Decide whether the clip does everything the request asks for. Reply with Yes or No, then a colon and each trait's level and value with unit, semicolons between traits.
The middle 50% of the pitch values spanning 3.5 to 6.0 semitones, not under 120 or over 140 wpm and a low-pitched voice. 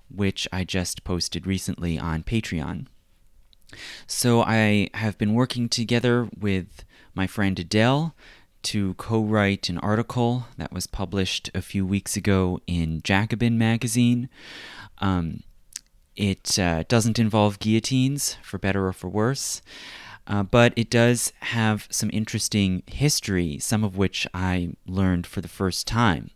Yes: average, 3.9 semitones; slow, 135 wpm; low, 100 Hz